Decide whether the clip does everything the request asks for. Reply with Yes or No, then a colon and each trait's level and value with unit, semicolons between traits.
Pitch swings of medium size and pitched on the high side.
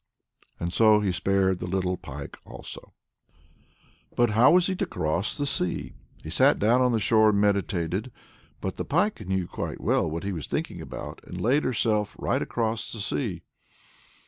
No: average, 4.1 semitones; low, 105 Hz